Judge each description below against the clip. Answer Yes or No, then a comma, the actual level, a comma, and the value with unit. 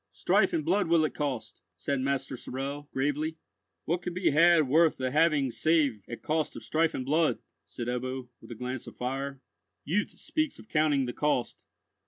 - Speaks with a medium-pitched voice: Yes, medium, 145 Hz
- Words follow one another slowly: No, average, 185 wpm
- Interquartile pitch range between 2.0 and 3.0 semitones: No, average, 3.8 semitones